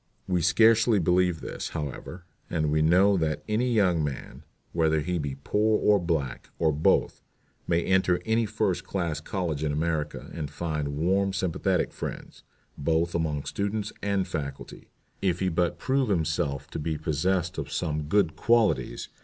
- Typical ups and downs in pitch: Yes, average, 4.0 semitones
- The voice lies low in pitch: Yes, very low, 85 Hz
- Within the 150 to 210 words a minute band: Yes, average, 155 wpm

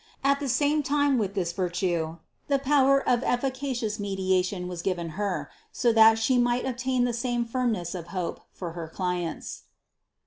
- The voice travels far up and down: Yes, wide, 6.2 semitones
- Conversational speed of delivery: Yes, average, 170 wpm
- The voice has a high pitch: Yes, high, 225 Hz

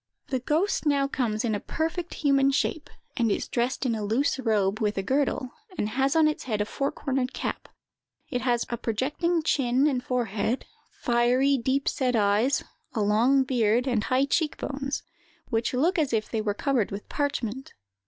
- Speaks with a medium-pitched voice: No, very high, 255 Hz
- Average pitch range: Yes, average, 3.7 semitones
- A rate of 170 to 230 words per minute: Yes, average, 185 wpm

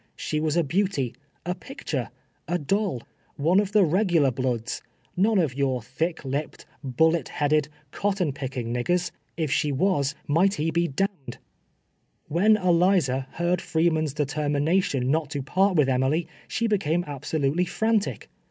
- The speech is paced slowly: No, average, 160 wpm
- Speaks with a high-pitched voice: No, medium, 160 Hz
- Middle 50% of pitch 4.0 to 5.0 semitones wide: Yes, average, 4.5 semitones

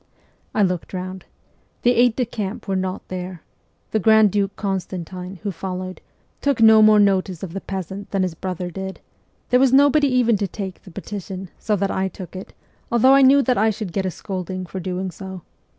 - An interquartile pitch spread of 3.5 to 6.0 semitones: No, average, 2.8 semitones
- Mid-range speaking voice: No, high, 195 Hz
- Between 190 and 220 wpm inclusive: Yes, average, 200 wpm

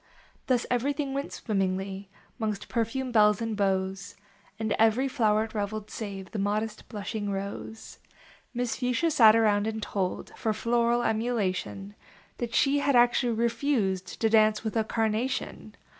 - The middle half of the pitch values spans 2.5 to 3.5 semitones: Yes, average, 2.8 semitones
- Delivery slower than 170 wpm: Yes, average, 140 wpm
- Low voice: No, high, 220 Hz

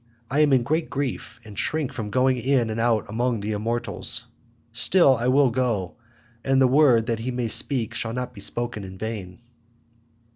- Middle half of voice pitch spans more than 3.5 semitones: No, average, 2.8 semitones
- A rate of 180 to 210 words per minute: Yes, average, 185 wpm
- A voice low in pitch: Yes, low, 120 Hz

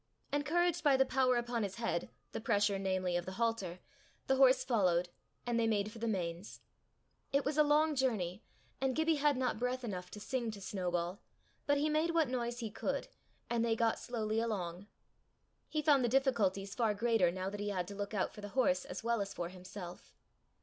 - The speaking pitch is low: No, high, 225 Hz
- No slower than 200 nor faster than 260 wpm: Yes, fast, 205 wpm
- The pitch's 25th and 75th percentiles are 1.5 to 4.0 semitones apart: No, average, 5.2 semitones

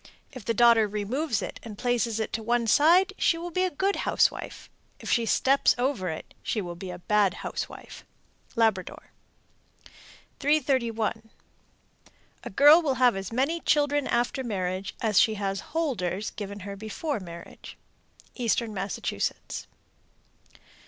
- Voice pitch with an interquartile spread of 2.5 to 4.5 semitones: No, wide, 5.5 semitones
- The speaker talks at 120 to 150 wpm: Yes, average, 140 wpm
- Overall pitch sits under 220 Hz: No, high, 230 Hz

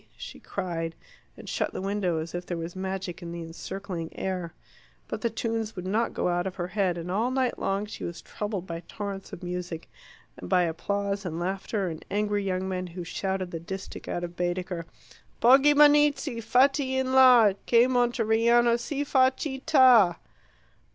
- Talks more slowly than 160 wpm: No, average, 175 wpm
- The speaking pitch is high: Yes, high, 195 Hz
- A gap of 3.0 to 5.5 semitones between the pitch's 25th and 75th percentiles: Yes, average, 5.1 semitones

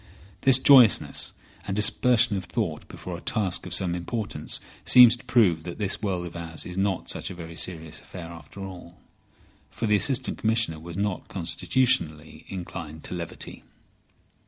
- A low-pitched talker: Yes, very low, 95 Hz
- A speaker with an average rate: Yes, average, 160 wpm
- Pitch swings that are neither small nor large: Yes, average, 4.6 semitones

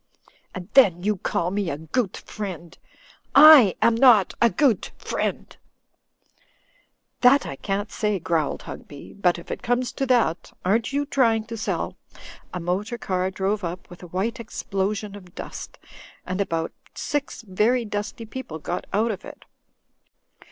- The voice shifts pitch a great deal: No, average, 4.4 semitones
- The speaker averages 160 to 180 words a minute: Yes, average, 165 wpm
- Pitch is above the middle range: Yes, high, 205 Hz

